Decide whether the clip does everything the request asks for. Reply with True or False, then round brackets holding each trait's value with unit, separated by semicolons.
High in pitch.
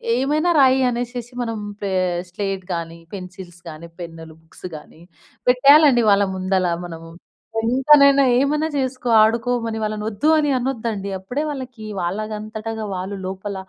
True (220 Hz)